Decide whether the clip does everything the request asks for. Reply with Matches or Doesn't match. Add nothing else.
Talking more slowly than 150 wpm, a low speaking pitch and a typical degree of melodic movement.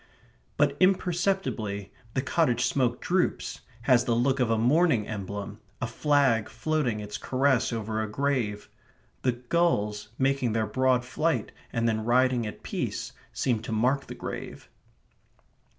Matches